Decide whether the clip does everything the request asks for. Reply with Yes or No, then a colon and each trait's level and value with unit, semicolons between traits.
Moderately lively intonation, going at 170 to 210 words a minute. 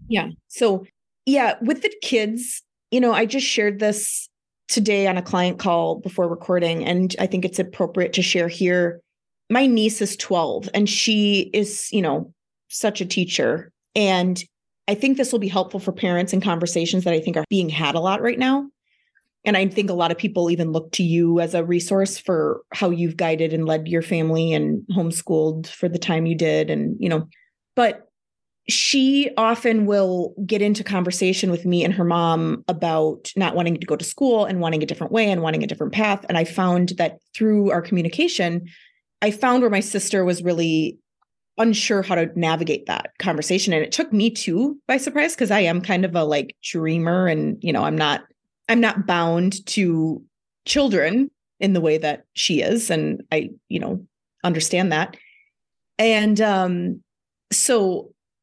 Yes: average, 3.9 semitones; average, 185 wpm